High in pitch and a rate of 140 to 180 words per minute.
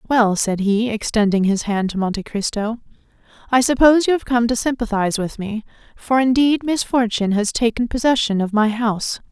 Yes: high, 225 Hz; average, 175 wpm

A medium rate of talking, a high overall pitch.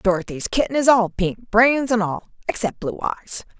Yes: average, 150 wpm; high, 220 Hz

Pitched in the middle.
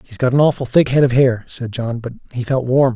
No: low, 125 Hz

